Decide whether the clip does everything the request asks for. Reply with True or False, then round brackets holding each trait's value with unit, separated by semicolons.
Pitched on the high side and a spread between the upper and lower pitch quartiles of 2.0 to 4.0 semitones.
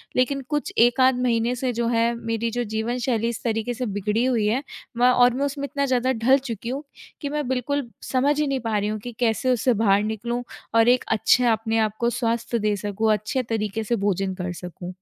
True (235 Hz; 2.6 semitones)